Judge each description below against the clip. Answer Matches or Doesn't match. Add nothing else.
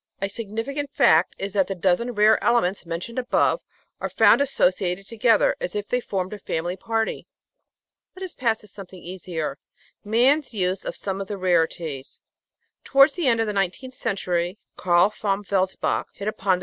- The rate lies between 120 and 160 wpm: Doesn't match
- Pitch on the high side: Matches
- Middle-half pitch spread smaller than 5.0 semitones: Matches